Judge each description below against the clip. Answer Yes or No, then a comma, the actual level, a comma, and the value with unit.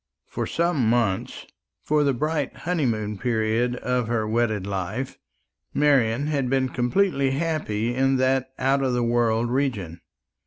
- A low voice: Yes, low, 125 Hz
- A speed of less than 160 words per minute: Yes, average, 140 wpm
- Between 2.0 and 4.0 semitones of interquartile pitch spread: Yes, average, 3.4 semitones